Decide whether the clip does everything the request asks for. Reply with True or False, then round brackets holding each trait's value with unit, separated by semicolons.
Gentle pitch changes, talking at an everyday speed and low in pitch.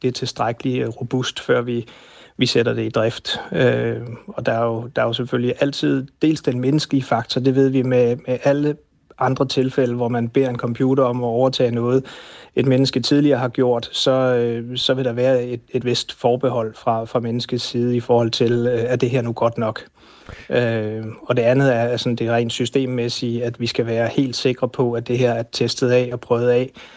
True (1.8 semitones; 215 wpm; 125 Hz)